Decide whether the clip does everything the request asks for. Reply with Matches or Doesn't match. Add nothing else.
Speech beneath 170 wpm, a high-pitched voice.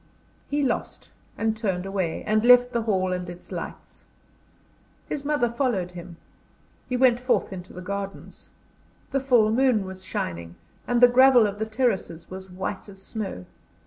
Matches